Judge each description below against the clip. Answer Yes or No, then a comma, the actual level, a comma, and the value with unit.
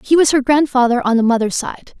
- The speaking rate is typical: No, fast, 240 wpm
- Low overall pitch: No, very high, 260 Hz